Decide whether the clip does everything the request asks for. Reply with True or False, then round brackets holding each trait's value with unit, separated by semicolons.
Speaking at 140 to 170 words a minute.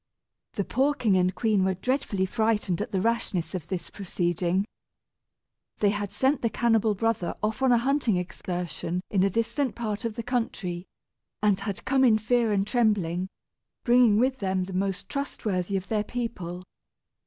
True (165 wpm)